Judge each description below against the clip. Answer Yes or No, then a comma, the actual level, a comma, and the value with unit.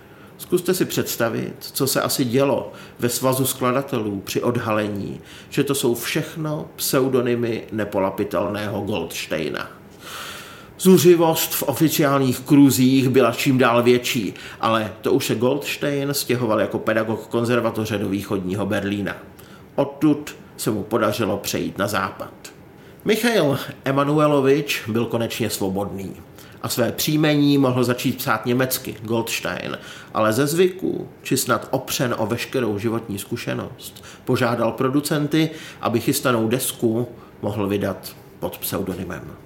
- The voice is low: Yes, low, 120 Hz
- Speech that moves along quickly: No, average, 120 wpm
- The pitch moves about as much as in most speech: Yes, average, 4.9 semitones